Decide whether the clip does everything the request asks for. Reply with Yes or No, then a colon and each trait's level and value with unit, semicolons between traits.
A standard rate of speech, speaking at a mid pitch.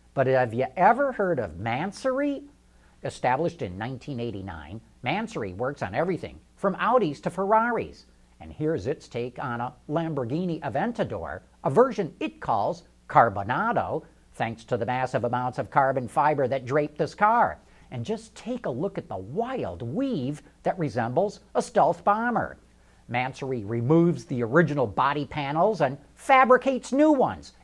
Yes: average, 145 wpm; medium, 145 Hz